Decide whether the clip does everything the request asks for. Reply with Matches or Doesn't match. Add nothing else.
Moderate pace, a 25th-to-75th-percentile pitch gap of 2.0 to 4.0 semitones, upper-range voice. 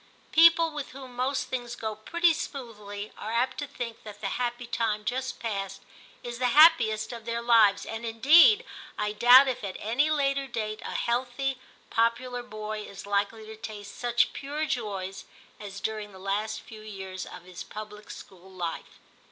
Matches